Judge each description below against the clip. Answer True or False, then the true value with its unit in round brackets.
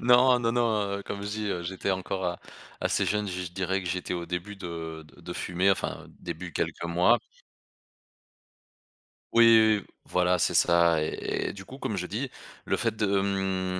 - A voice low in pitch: True (95 Hz)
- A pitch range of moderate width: True (3.0 semitones)